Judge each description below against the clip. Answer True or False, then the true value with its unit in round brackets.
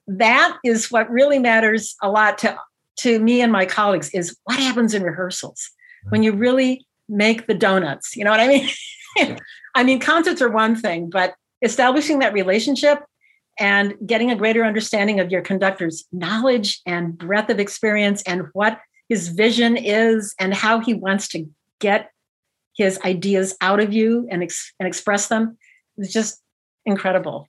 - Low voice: False (215 Hz)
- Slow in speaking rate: False (165 wpm)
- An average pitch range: True (3.3 semitones)